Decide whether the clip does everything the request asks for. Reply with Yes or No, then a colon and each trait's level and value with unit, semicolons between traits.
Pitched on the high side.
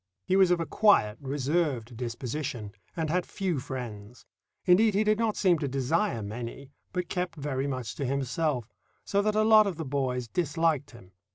No: medium, 145 Hz